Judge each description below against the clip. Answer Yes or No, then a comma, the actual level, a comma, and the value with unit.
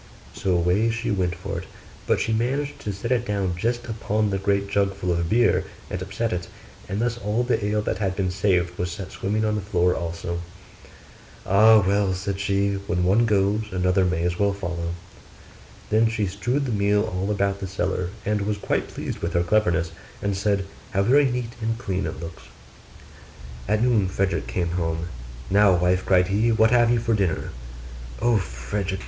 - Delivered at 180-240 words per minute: Yes, average, 190 wpm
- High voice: No, low, 100 Hz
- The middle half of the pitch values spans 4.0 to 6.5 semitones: No, average, 3.0 semitones